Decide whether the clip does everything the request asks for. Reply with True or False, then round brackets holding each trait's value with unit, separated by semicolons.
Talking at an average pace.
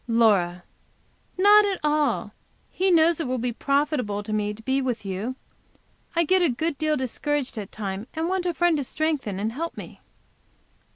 True (180 wpm)